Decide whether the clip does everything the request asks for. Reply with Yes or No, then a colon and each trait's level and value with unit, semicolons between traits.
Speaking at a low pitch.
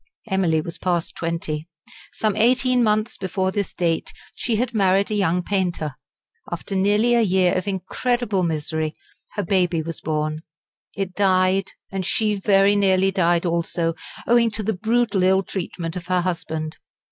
No: high, 190 Hz